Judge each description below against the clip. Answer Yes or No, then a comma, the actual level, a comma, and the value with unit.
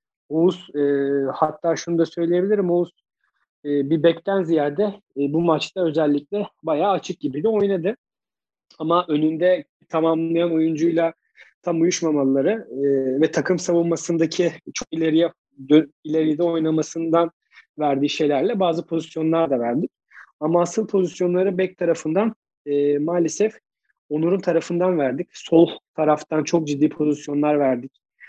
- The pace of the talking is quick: No, average, 115 wpm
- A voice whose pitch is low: No, medium, 165 Hz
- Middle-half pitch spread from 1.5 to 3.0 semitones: Yes, narrow, 2.5 semitones